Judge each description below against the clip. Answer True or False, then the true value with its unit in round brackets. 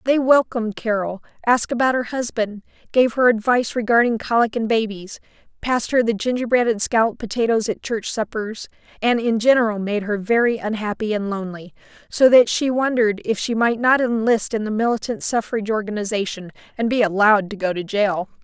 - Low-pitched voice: False (225 Hz)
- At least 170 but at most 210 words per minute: True (175 wpm)